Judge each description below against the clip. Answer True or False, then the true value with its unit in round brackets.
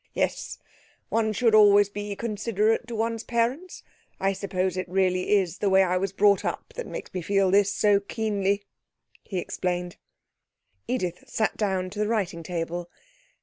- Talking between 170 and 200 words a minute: False (160 wpm)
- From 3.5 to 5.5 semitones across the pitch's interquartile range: False (2.8 semitones)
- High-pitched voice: True (200 Hz)